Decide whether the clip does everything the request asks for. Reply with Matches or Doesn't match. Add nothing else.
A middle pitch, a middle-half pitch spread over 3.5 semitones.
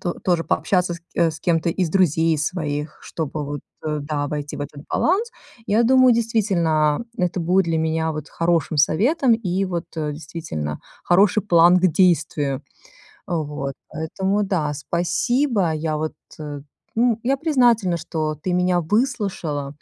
Matches